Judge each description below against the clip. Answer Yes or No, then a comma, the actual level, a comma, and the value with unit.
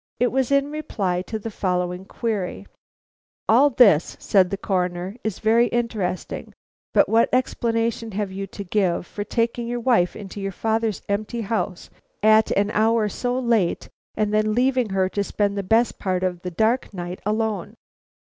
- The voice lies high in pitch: Yes, high, 215 Hz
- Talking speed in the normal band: Yes, average, 165 wpm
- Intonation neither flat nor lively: Yes, average, 3.4 semitones